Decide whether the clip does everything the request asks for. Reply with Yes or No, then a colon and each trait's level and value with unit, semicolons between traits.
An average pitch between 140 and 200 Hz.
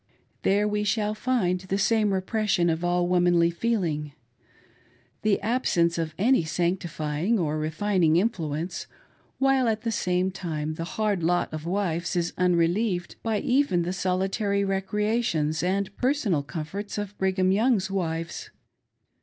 Yes: medium, 185 Hz